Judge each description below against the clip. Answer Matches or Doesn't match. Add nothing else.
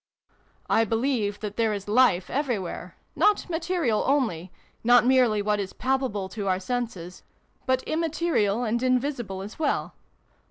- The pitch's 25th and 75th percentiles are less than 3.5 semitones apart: Doesn't match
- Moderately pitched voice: Doesn't match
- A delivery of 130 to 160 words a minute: Matches